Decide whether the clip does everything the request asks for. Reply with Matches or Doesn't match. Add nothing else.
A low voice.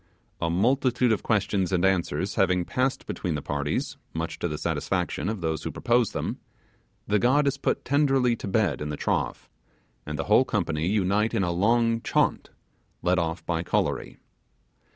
Matches